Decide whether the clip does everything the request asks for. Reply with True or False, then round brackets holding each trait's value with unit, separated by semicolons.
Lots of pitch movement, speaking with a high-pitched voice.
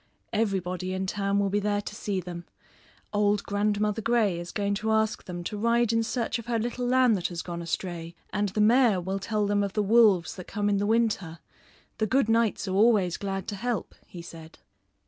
False (2.9 semitones; 205 Hz)